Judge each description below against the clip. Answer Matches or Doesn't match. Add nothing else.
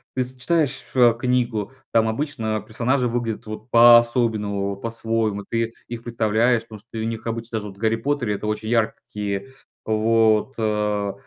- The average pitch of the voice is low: Matches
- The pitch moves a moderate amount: Doesn't match